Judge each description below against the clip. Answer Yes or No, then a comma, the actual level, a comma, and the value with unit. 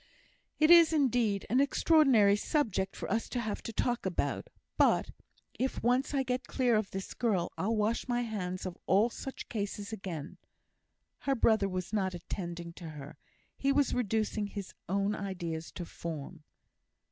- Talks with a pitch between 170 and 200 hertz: No, high, 210 Hz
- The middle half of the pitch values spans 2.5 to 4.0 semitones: No, average, 4.9 semitones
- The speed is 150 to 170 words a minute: Yes, average, 160 wpm